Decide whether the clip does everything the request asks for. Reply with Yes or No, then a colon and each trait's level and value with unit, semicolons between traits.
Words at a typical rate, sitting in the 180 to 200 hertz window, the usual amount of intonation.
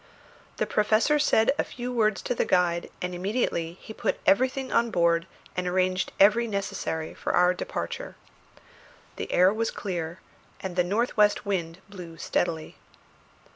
Yes: average, 150 wpm; high, 190 Hz; average, 3.9 semitones